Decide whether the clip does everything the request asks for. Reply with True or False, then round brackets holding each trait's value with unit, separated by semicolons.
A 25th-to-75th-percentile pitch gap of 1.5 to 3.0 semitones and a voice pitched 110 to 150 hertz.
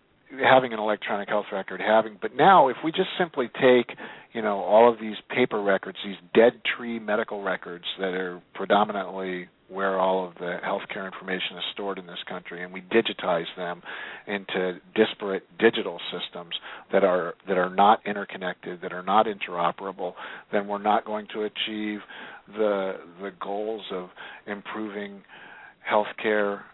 False (2.4 semitones; 100 Hz)